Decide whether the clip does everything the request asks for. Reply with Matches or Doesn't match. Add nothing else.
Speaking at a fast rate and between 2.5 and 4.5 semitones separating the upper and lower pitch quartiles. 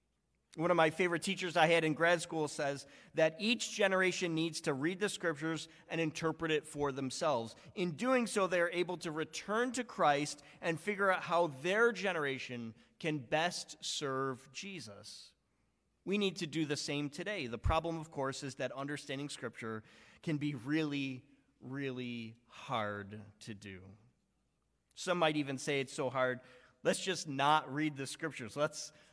Doesn't match